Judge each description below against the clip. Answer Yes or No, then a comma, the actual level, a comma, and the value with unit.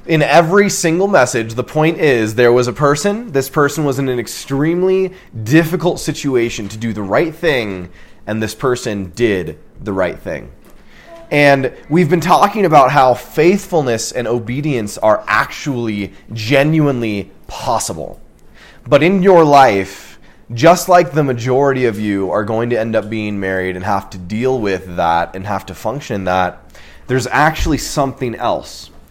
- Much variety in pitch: Yes, wide, 7.0 semitones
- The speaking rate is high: No, average, 155 wpm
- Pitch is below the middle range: Yes, low, 125 Hz